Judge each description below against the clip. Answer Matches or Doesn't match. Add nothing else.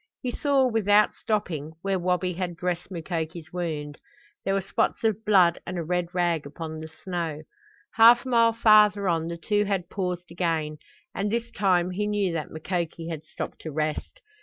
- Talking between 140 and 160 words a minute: Doesn't match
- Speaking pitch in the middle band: Matches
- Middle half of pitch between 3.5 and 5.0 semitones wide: Matches